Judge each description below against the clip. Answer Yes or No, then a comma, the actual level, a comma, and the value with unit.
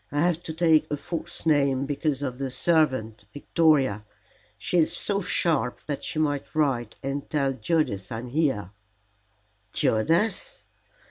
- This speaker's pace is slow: No, average, 145 wpm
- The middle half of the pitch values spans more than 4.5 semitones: No, average, 3.7 semitones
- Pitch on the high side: No, medium, 145 Hz